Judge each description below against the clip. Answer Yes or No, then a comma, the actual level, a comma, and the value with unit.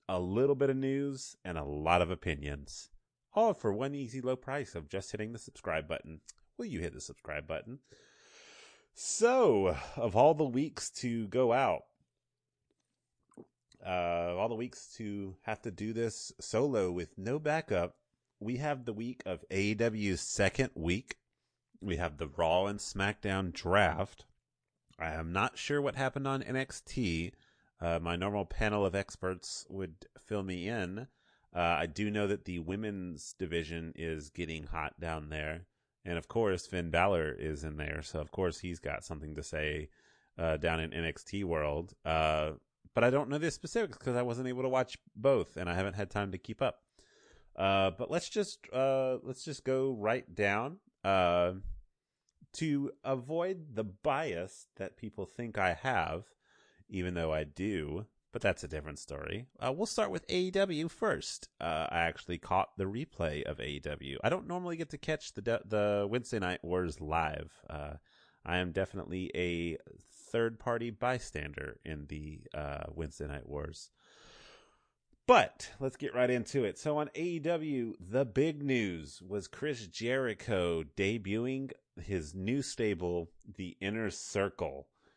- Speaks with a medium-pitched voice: No, low, 100 Hz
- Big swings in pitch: Yes, wide, 7.4 semitones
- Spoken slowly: No, average, 165 wpm